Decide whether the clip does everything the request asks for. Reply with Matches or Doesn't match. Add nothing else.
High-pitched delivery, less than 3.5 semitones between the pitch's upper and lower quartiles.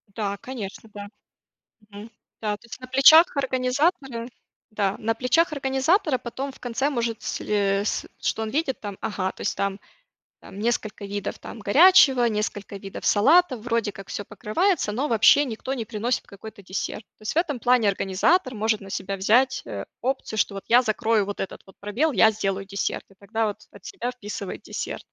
Doesn't match